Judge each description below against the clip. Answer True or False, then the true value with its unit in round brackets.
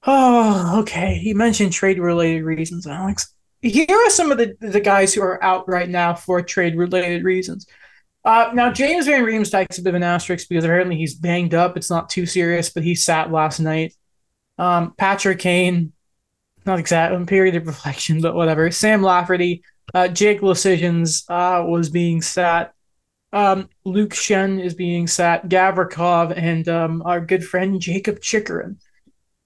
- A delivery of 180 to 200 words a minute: False (160 wpm)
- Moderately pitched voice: True (180 Hz)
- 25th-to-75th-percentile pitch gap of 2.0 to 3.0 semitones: True (2.4 semitones)